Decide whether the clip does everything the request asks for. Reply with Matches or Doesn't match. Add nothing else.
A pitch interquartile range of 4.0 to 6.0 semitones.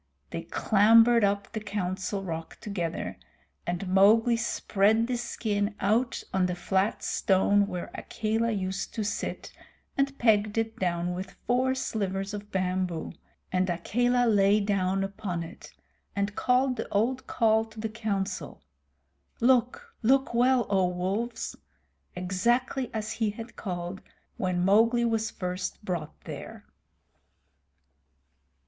Doesn't match